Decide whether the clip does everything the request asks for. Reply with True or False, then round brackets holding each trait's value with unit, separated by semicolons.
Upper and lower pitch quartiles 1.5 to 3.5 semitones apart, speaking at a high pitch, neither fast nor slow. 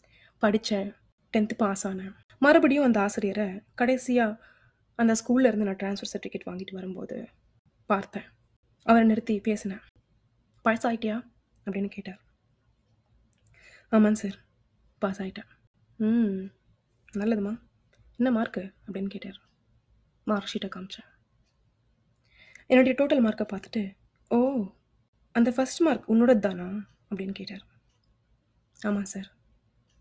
True (2.9 semitones; 205 Hz; 100 wpm)